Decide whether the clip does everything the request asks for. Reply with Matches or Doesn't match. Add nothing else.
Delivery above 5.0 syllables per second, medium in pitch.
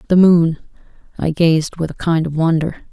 Matches